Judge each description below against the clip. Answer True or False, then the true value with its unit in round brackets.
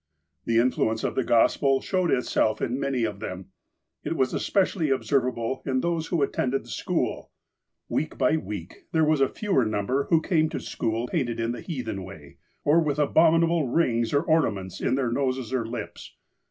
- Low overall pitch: True (130 Hz)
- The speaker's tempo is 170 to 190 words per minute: True (185 wpm)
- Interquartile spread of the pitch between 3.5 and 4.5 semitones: False (5.3 semitones)